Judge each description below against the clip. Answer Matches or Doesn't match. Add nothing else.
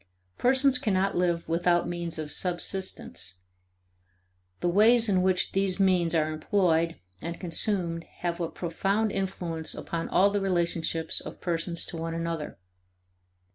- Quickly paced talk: Doesn't match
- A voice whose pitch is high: Doesn't match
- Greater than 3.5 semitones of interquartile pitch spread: Doesn't match